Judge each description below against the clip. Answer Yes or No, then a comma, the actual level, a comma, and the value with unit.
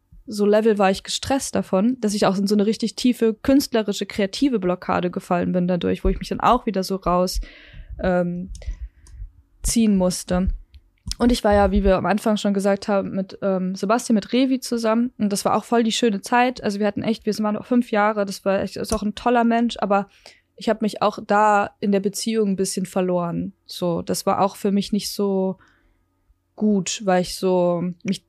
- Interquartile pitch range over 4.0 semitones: No, average, 3.0 semitones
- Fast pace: Yes, fast, 210 wpm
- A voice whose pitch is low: No, high, 200 Hz